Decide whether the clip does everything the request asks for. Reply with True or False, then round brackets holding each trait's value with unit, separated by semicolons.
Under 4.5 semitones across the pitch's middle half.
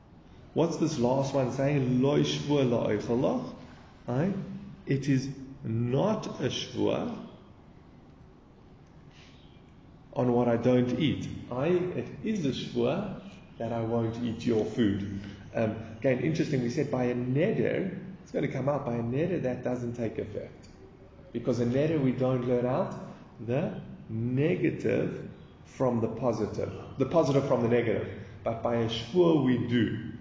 True (3.6 semitones)